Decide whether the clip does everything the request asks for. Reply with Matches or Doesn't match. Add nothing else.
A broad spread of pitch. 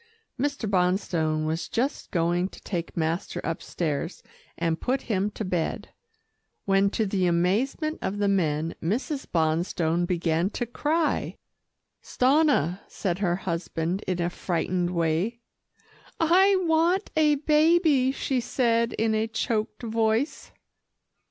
Matches